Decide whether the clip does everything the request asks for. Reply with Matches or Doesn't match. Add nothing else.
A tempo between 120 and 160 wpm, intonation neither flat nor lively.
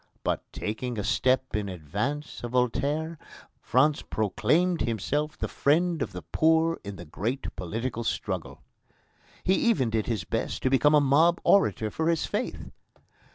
Doesn't match